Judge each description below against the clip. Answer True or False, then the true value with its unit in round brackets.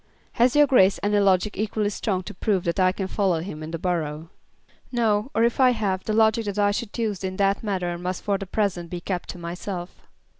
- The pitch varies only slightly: False (3.0 semitones)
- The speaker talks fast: True (225 wpm)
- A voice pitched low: False (195 Hz)